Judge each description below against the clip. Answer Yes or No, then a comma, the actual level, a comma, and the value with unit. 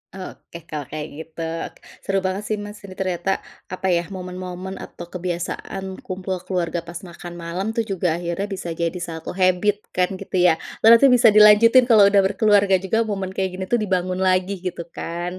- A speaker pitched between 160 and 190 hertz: Yes, medium, 185 Hz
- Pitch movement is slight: Yes, narrow, 2.3 semitones